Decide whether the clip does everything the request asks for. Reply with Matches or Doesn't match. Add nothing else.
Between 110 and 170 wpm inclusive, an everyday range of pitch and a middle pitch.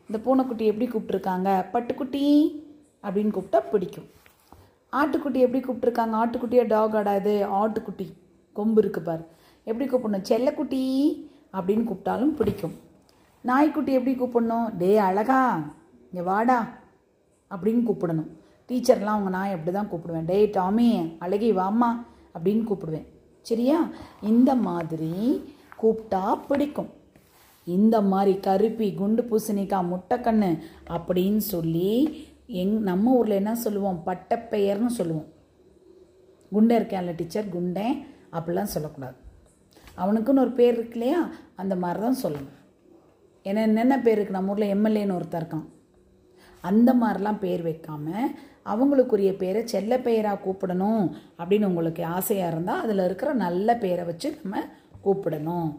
Doesn't match